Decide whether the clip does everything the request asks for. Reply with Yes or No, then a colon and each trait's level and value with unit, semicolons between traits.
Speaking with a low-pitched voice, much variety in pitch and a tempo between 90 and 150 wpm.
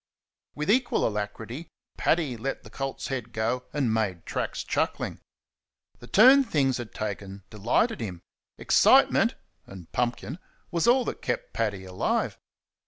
Yes: low, 120 Hz; wide, 6.2 semitones; slow, 135 wpm